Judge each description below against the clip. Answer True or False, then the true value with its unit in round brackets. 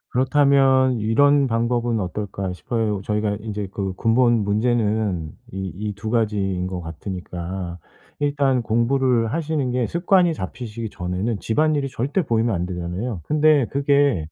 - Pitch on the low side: True (115 Hz)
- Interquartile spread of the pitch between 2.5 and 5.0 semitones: False (5.4 semitones)